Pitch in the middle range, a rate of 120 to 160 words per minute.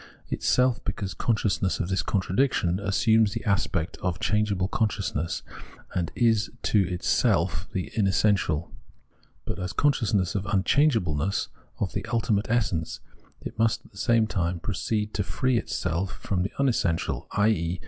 No: low, 100 Hz; average, 140 wpm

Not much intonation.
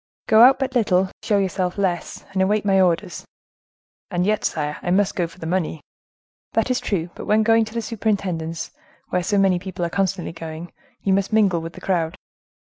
No: average, 3.4 semitones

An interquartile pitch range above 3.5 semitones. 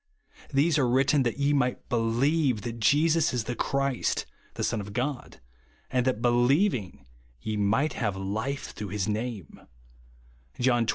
Yes: average, 4.0 semitones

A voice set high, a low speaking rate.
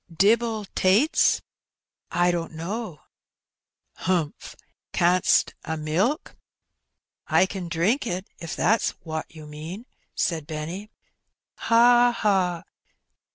No: medium, 180 Hz; slow, 110 wpm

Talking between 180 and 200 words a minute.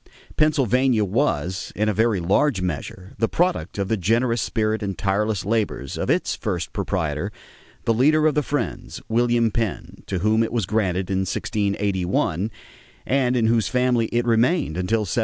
No: average, 165 wpm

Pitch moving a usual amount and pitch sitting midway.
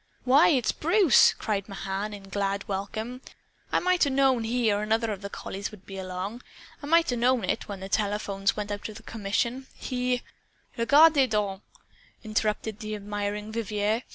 No: average, 3.7 semitones; high, 215 Hz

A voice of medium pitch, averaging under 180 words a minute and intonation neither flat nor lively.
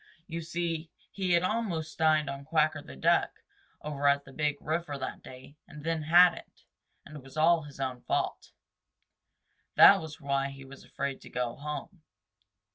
Yes: medium, 150 Hz; average, 170 wpm; average, 3.1 semitones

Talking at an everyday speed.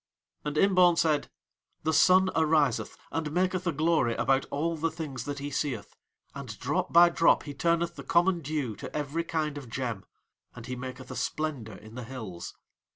Yes: average, 180 wpm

